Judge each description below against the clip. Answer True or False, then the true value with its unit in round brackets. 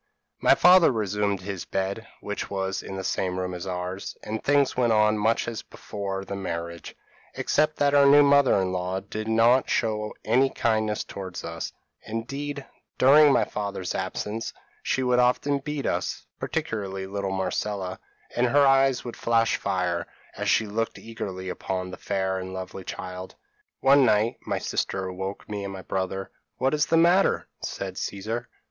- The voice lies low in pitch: True (105 Hz)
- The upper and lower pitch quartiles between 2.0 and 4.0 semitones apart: False (4.9 semitones)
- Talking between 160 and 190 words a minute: True (170 wpm)